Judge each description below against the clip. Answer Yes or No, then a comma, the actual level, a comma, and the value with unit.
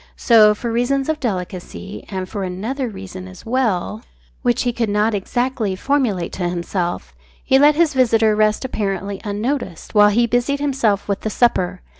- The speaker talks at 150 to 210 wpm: Yes, average, 165 wpm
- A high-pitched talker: Yes, high, 215 Hz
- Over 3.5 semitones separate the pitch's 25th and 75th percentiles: Yes, average, 4.6 semitones